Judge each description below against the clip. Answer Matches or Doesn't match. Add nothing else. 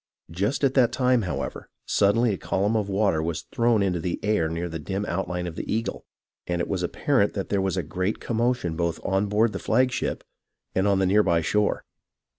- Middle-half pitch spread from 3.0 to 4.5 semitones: Matches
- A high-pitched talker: Doesn't match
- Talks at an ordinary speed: Doesn't match